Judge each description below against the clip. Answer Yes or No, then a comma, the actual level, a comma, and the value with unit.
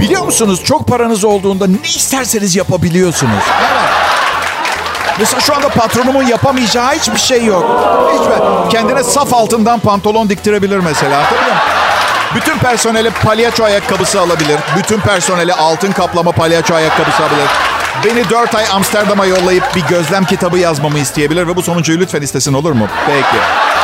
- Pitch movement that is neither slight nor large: Yes, average, 4.7 semitones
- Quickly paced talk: Yes, fast, 145 wpm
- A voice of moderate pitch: No, high, 195 Hz